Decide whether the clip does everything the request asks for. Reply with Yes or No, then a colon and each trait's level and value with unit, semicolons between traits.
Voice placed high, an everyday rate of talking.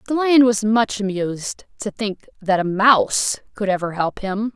Yes: high, 210 Hz; average, 185 wpm